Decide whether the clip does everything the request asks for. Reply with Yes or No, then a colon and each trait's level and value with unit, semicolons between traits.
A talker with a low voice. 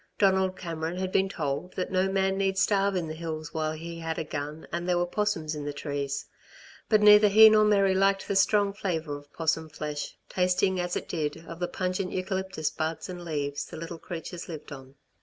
No: medium, 175 Hz